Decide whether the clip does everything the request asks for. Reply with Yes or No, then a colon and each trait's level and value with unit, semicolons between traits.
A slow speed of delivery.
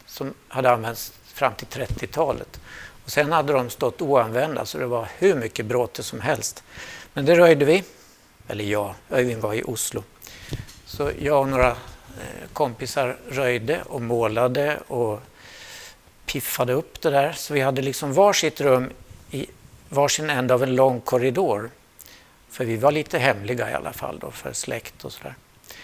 No: average, 160 wpm